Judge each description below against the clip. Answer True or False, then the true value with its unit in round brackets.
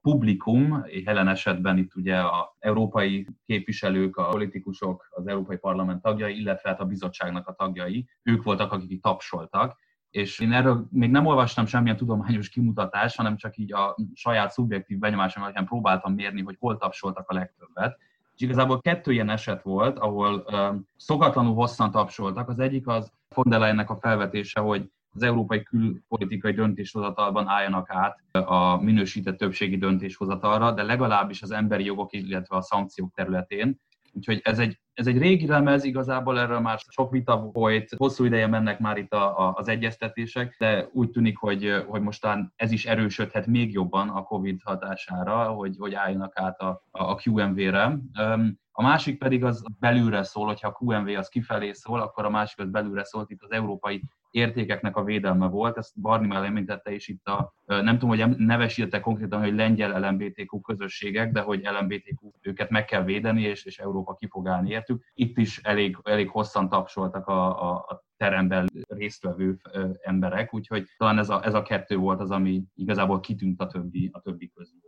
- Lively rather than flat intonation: False (2.7 semitones)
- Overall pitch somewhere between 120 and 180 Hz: False (105 Hz)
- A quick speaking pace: True (170 wpm)